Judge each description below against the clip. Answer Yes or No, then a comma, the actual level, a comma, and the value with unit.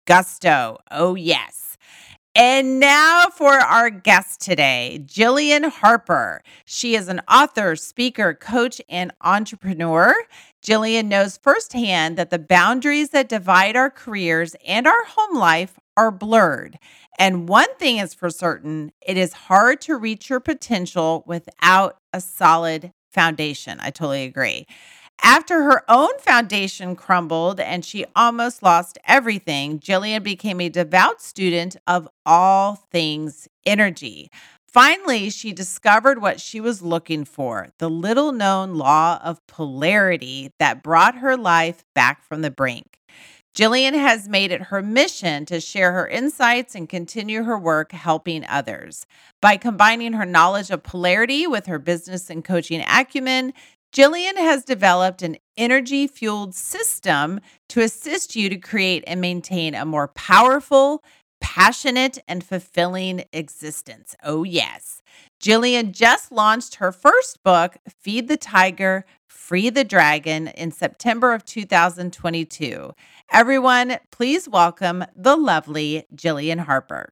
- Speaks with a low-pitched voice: No, high, 190 Hz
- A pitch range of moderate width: No, wide, 6.1 semitones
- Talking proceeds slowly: Yes, slow, 130 wpm